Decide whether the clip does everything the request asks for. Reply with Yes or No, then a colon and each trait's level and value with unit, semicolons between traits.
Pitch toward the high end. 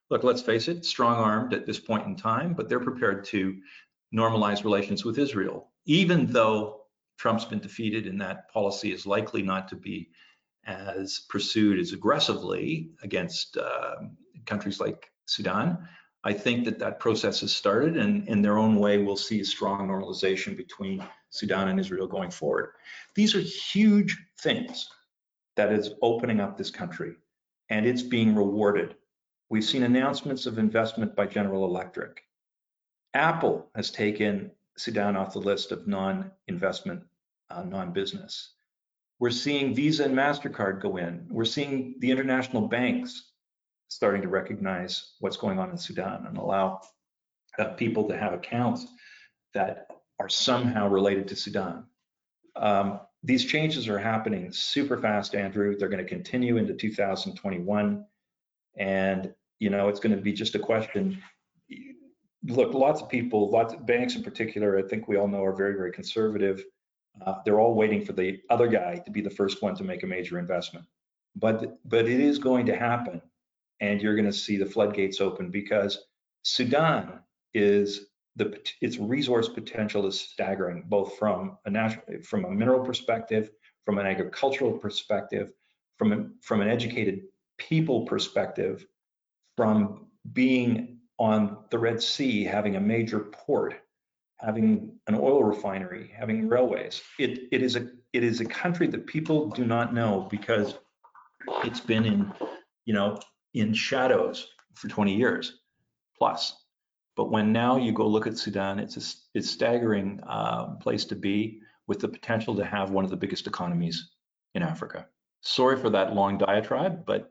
No: low, 110 Hz